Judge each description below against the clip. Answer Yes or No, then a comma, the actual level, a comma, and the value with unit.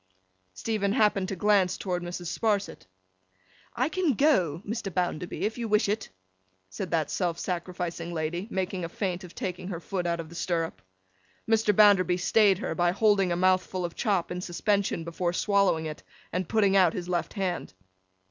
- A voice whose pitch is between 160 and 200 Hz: Yes, medium, 185 Hz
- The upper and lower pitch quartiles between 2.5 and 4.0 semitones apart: Yes, average, 2.8 semitones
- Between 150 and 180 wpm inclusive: Yes, average, 175 wpm